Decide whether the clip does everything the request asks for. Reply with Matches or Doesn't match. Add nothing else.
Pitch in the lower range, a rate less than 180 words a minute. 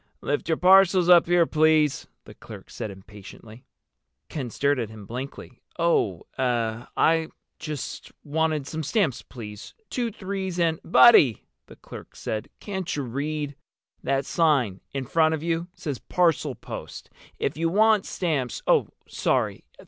Doesn't match